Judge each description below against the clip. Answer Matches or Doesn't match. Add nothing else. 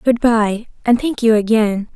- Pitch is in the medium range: Doesn't match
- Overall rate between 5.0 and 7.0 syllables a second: Doesn't match